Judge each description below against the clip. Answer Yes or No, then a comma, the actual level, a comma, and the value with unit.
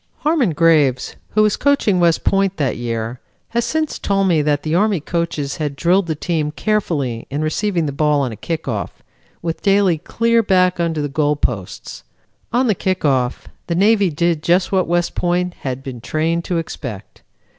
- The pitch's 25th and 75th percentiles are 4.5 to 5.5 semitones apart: Yes, average, 4.9 semitones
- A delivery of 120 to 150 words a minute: No, average, 185 wpm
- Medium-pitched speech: Yes, medium, 165 Hz